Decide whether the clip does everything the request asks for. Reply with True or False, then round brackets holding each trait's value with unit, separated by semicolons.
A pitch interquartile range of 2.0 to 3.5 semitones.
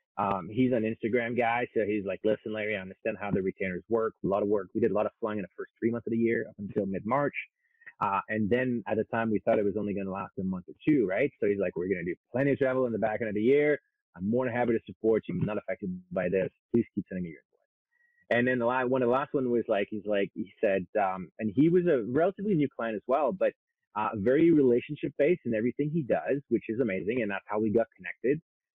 False (4.8 semitones)